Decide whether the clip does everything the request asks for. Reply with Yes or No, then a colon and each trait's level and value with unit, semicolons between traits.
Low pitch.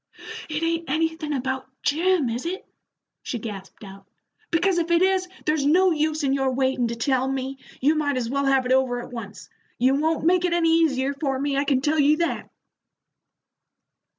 No: very high, 280 Hz